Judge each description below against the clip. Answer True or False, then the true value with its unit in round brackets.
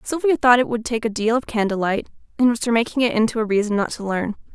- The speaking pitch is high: True (230 Hz)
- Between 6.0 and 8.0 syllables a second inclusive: True (6.5 syllables/s)